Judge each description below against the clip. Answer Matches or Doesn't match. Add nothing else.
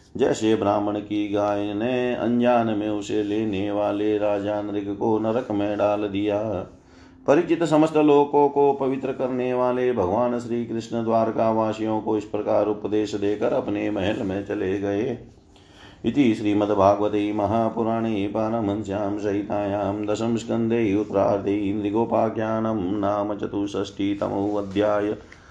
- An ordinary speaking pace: Matches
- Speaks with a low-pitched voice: Matches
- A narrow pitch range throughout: Matches